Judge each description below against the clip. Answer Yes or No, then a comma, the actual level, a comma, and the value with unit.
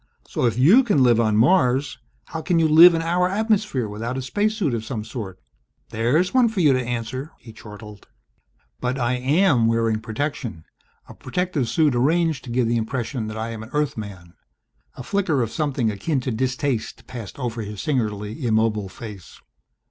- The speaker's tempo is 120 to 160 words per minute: No, average, 180 wpm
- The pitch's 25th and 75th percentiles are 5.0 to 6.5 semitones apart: Yes, wide, 5.6 semitones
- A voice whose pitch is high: No, low, 125 Hz